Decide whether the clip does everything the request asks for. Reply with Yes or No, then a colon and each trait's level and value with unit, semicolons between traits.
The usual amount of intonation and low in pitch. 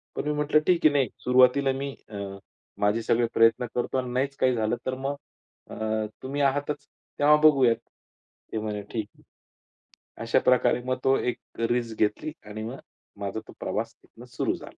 Yes: average, 3.4 semitones; low, 130 Hz